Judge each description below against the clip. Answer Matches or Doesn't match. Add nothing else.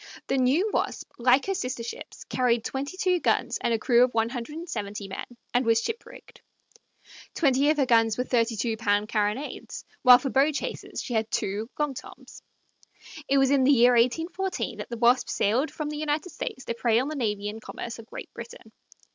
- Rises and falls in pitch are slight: Doesn't match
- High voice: Matches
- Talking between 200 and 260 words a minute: Matches